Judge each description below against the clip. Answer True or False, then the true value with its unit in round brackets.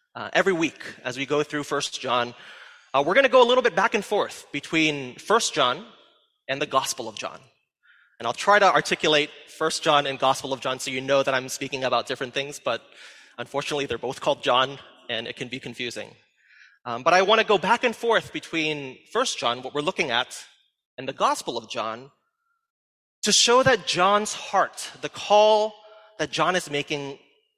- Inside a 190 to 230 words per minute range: True (200 wpm)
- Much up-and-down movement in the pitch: True (7.8 semitones)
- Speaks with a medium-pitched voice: True (155 Hz)